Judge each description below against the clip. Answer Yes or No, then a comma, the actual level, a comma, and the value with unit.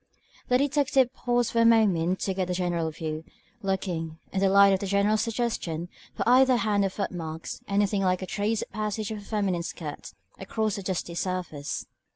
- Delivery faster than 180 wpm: Yes, average, 195 wpm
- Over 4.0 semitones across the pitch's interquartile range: No, average, 3.7 semitones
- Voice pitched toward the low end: No, high, 195 Hz